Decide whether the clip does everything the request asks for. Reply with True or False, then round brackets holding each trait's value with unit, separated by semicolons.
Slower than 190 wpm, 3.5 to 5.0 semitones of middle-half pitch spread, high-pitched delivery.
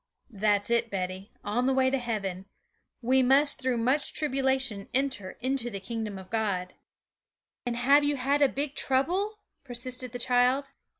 True (160 wpm; 4.0 semitones; 250 Hz)